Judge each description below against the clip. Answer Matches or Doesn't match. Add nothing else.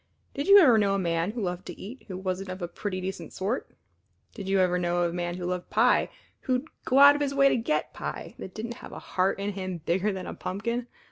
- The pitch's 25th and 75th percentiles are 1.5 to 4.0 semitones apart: Doesn't match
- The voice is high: Matches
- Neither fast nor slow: Doesn't match